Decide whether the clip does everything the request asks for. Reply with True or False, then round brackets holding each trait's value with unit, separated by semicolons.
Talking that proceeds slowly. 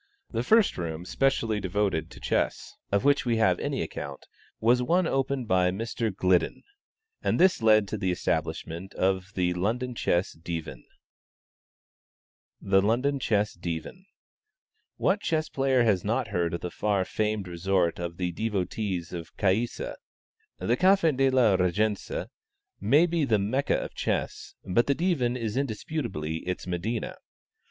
False (145 wpm)